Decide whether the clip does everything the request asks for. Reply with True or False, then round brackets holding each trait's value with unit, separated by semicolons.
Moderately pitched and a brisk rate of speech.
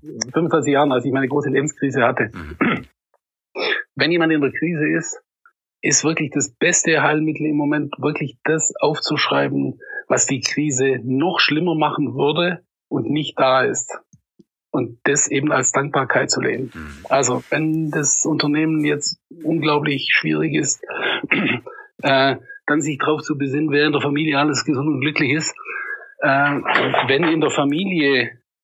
False (150 Hz; 150 wpm)